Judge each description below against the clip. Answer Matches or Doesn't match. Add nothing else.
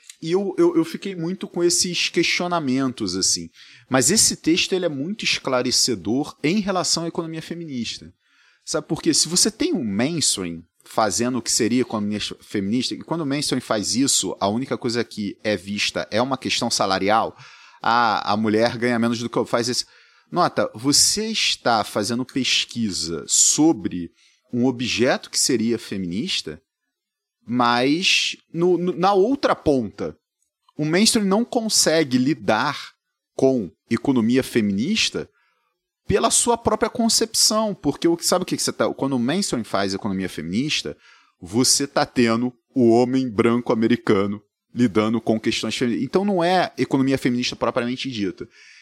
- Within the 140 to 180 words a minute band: Matches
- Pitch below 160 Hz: Matches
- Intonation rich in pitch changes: Matches